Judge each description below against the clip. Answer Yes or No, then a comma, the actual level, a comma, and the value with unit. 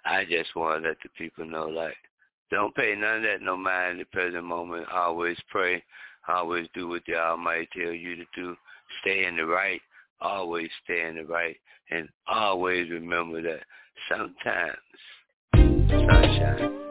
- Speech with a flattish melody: Yes, narrow, 1.4 semitones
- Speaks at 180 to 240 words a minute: No, average, 165 wpm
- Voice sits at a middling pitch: No, very low, 85 Hz